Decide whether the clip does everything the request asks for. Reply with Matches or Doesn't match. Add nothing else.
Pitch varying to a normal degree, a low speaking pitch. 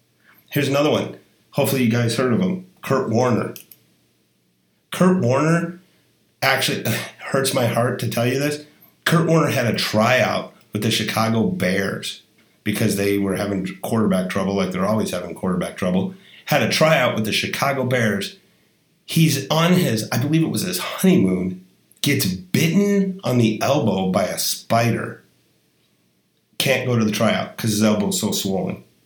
Doesn't match